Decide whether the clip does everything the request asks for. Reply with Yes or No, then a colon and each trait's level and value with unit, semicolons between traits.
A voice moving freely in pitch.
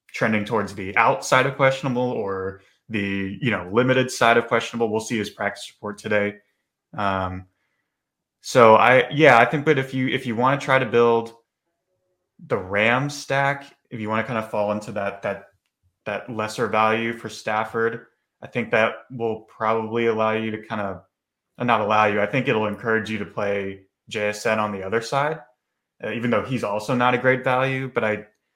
No: average, 3.3 semitones